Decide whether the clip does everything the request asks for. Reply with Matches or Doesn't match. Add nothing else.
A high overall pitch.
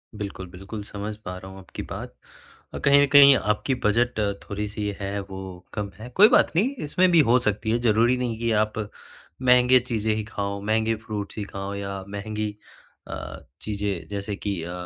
Doesn't match